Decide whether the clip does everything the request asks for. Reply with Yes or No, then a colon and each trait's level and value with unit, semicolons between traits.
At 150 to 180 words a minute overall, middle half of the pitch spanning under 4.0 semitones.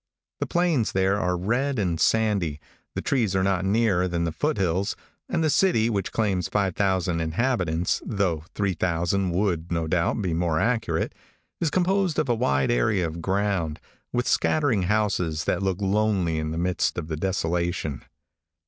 No: average, 165 wpm; average, 4.3 semitones